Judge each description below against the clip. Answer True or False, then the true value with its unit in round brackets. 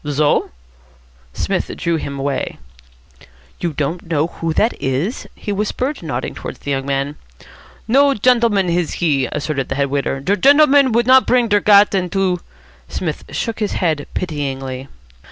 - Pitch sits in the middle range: True (170 Hz)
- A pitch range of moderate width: False (7.1 semitones)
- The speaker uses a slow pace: False (155 wpm)